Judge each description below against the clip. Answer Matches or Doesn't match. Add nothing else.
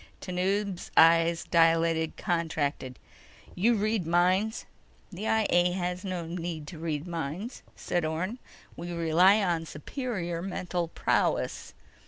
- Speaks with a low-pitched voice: Doesn't match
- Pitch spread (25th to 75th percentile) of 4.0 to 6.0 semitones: Doesn't match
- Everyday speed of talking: Doesn't match